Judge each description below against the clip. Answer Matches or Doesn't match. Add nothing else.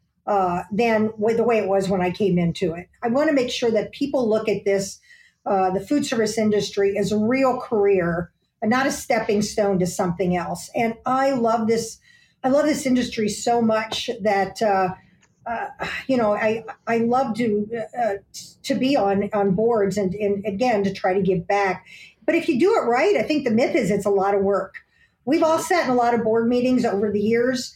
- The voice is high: Matches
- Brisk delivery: Matches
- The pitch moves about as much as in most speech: Matches